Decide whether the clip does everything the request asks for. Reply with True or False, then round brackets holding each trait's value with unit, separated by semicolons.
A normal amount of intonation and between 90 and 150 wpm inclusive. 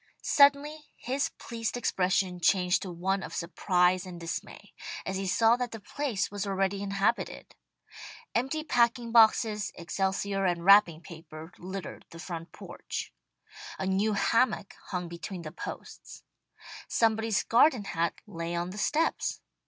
True (4.3 semitones; 135 wpm)